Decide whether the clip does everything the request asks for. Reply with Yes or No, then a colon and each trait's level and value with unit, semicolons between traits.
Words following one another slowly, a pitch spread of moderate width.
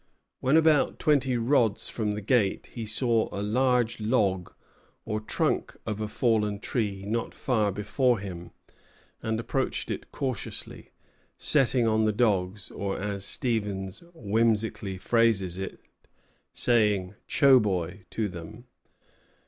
Yes: slow, 125 wpm; average, 3.1 semitones